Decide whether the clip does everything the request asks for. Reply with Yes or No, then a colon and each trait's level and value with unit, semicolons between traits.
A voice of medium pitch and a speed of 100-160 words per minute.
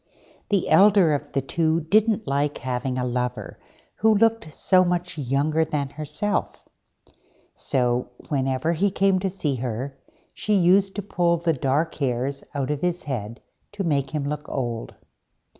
Yes: medium, 150 Hz; average, 155 wpm